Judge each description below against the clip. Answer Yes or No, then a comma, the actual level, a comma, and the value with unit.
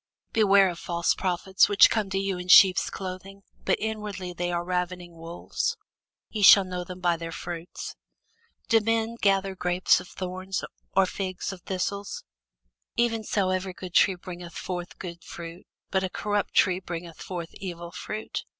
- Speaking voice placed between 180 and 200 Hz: Yes, medium, 185 Hz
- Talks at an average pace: Yes, average, 165 wpm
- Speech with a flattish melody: Yes, narrow, 1.9 semitones